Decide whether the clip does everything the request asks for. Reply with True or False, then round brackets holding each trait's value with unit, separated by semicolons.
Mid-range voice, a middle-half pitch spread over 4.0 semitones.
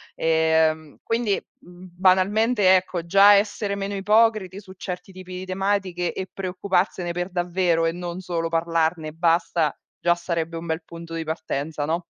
False (180 Hz; 2.5 semitones)